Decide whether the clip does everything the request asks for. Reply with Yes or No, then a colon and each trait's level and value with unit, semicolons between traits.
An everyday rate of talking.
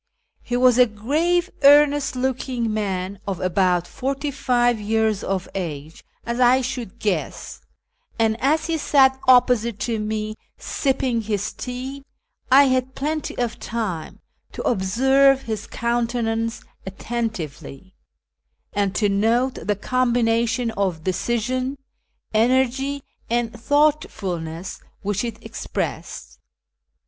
No: slow, 115 wpm